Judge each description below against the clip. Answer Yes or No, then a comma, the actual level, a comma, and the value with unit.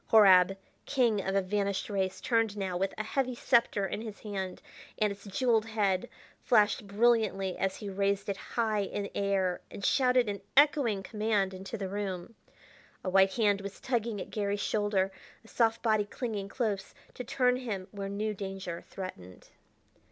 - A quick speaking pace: No, average, 165 wpm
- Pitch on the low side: No, high, 205 Hz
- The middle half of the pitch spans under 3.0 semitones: Yes, narrow, 2.5 semitones